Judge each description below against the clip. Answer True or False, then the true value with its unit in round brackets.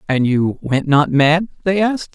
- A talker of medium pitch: True (160 Hz)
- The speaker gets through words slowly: False (195 wpm)